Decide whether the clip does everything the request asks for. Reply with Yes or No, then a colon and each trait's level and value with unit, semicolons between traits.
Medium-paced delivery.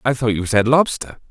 No: fast, 230 wpm